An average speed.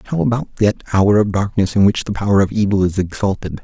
No: fast, 230 wpm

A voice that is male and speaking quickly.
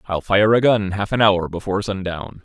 Yes: male; fast, 220 wpm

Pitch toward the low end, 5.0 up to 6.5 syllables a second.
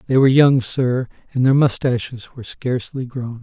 Yes: low, 125 Hz; 5.5 syllables/s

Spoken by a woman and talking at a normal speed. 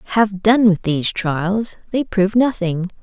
Yes: female; average, 160 wpm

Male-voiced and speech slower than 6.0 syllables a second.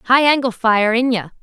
No: female; 4.6 syllables/s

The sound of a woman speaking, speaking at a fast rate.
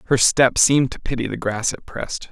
No: male; fast, 235 wpm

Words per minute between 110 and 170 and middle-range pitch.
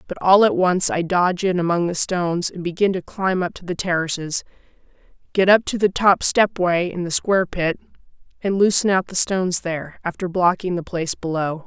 No: fast, 205 wpm; medium, 180 Hz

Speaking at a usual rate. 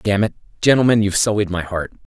Yes: average, 195 wpm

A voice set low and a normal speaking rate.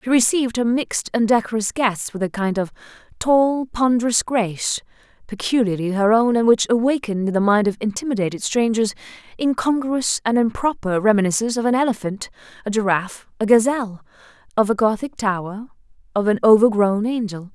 No: high, 220 Hz; average, 150 wpm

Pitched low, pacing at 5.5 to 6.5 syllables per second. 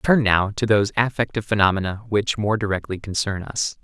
Yes: low, 105 Hz; 5.8 syllables/s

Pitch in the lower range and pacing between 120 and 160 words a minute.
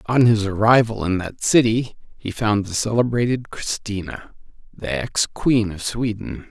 Yes: low, 110 Hz; average, 150 wpm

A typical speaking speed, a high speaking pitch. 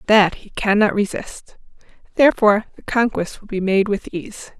Yes: average, 155 wpm; high, 205 Hz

